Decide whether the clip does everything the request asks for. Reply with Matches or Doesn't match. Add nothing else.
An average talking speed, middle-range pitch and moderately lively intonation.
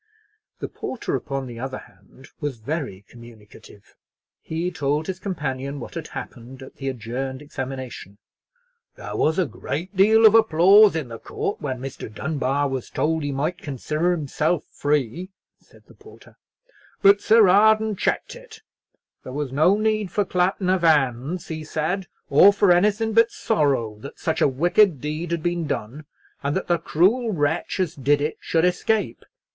Doesn't match